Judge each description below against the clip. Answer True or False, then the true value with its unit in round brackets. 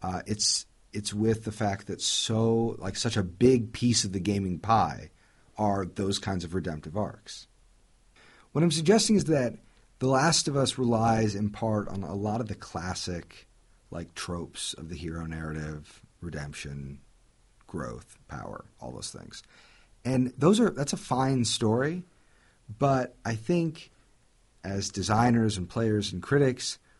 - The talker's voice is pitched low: True (110 Hz)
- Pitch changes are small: False (4.9 semitones)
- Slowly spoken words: False (155 wpm)